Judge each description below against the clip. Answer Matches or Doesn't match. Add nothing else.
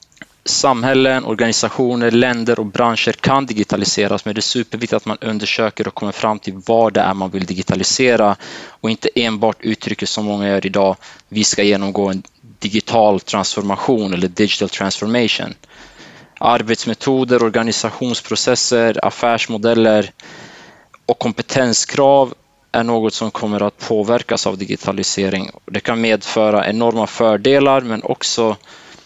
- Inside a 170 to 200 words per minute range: Doesn't match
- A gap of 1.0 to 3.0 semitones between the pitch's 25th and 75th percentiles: Matches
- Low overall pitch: Matches